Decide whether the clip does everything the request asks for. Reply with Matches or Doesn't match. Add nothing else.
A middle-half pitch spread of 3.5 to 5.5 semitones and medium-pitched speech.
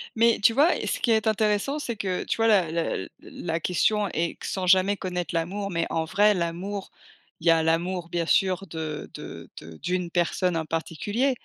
Matches